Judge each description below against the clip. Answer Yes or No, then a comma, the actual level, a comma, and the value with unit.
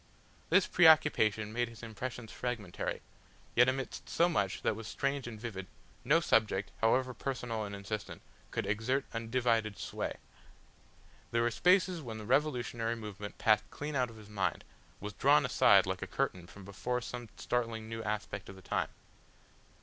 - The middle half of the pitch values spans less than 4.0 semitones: Yes, average, 3.1 semitones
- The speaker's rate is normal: Yes, average, 160 wpm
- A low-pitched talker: Yes, low, 115 Hz